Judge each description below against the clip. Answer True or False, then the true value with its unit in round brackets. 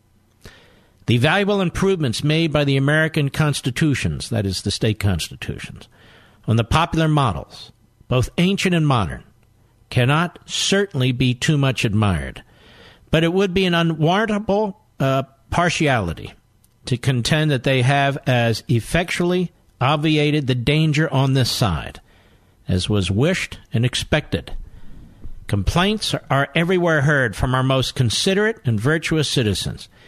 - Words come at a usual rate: False (130 wpm)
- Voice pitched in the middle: False (130 Hz)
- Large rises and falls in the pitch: True (6.3 semitones)